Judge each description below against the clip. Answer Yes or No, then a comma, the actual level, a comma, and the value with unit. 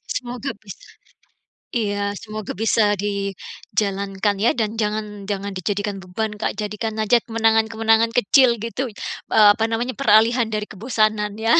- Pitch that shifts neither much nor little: No, narrow, 1.9 semitones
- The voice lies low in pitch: No, high, 215 Hz